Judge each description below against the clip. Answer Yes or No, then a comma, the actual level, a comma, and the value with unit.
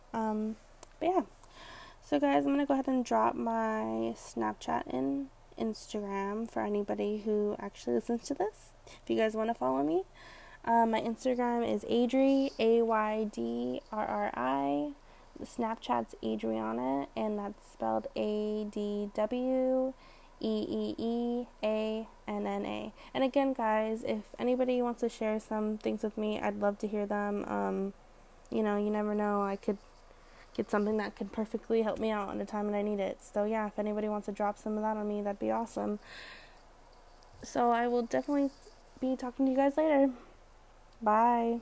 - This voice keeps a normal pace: Yes, average, 175 wpm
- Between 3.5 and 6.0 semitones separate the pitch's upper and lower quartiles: No, average, 2.8 semitones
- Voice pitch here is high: Yes, high, 215 Hz